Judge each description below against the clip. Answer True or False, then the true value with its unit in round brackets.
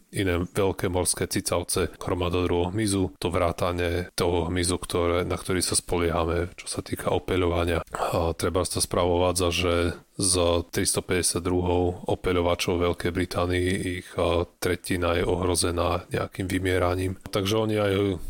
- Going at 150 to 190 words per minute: False (120 wpm)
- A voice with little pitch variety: True (1.2 semitones)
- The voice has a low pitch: True (90 Hz)